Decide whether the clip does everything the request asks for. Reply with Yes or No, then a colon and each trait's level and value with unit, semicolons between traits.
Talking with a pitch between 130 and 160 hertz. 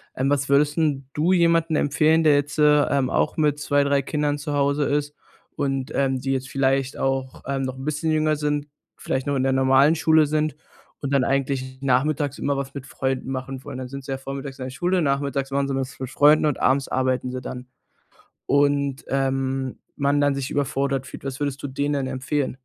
Yes: medium, 140 Hz